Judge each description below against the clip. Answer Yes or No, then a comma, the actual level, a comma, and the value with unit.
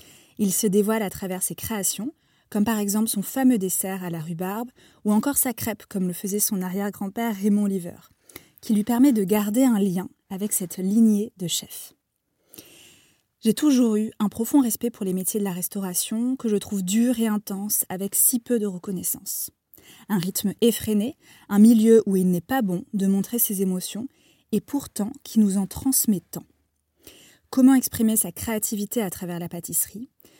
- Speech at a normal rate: Yes, average, 180 wpm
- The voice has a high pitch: Yes, high, 210 Hz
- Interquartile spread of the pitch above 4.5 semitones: No, average, 3.2 semitones